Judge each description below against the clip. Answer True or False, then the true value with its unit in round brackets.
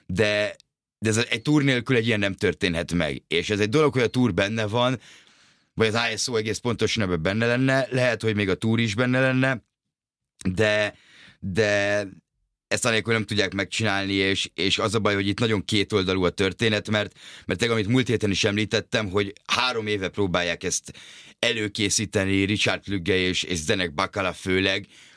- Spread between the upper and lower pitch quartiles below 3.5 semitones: True (2.8 semitones)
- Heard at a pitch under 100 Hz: False (105 Hz)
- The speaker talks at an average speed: False (175 wpm)